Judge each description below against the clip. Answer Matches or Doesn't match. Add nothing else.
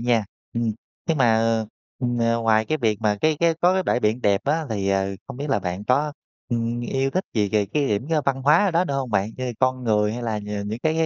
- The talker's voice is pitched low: Matches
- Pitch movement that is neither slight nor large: Matches